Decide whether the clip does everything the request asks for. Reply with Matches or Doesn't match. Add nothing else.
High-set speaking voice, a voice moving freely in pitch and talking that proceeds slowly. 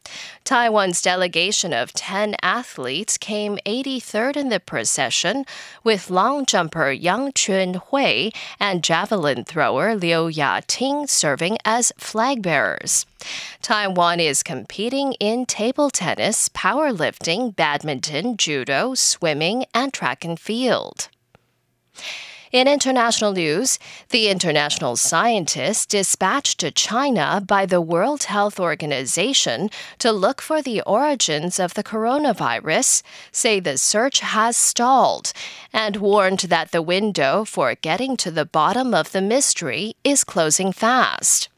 Matches